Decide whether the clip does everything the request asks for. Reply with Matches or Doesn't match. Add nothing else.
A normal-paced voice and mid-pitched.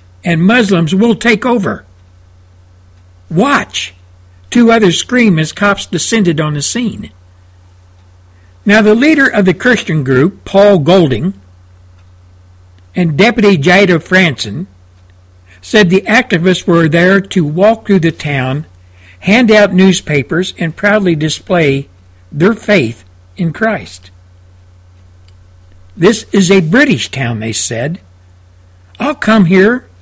Doesn't match